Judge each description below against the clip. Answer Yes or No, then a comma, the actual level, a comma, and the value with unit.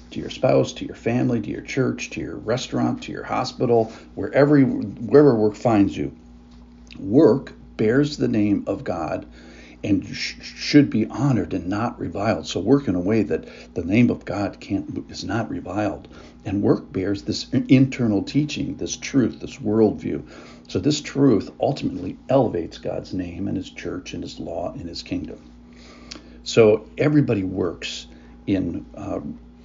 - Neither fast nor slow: Yes, average, 160 wpm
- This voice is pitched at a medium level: No, low, 100 Hz